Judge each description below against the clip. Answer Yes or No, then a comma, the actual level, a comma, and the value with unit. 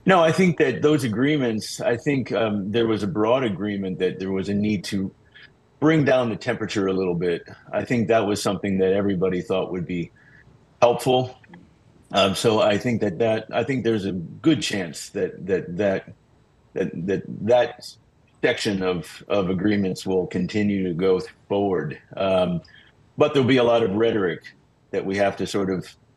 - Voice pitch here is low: Yes, low, 105 Hz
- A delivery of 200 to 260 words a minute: No, average, 180 wpm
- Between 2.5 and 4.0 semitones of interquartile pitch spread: No, average, 4.4 semitones